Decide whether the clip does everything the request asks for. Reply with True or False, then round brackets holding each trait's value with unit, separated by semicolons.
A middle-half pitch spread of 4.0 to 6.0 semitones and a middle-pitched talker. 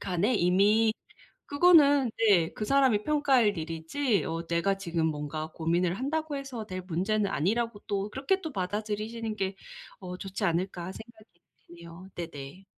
False (5.4 semitones; 200 Hz)